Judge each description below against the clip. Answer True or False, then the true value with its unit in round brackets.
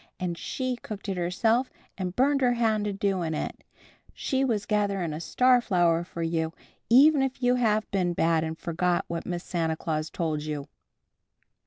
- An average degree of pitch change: False (6.1 semitones)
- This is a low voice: False (185 Hz)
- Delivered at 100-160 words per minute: False (175 wpm)